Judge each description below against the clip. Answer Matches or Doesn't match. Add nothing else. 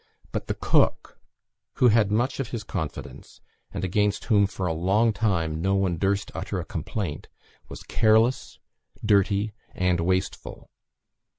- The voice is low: Matches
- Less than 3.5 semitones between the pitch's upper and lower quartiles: Matches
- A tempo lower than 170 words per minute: Matches